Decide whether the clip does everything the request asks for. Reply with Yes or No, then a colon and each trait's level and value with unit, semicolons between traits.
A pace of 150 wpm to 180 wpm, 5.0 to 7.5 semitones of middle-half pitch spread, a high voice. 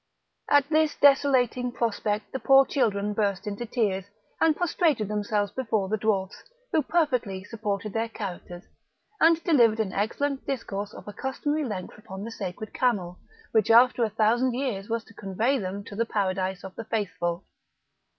No: average, 160 wpm; average, 4.3 semitones; high, 220 Hz